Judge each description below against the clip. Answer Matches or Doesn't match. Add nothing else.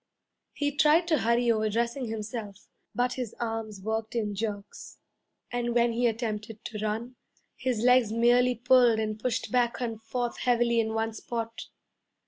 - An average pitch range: Doesn't match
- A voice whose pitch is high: Matches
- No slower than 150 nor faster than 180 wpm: Matches